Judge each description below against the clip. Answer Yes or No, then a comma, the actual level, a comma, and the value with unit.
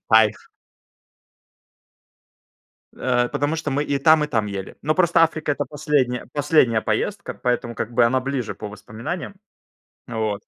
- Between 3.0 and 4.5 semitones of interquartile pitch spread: No, average, 5.0 semitones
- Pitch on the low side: Yes, low, 130 Hz